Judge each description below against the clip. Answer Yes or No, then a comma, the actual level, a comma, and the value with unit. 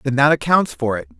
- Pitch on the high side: No, low, 125 Hz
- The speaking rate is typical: No, fast, 250 wpm